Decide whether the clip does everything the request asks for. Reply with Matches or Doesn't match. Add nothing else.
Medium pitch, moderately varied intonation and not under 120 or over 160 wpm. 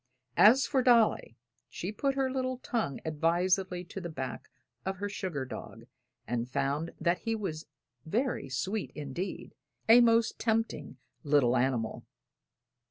Doesn't match